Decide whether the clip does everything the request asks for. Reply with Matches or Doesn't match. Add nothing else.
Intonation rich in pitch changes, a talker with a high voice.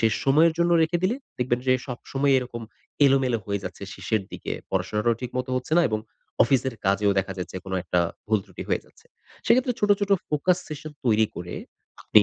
Doesn't match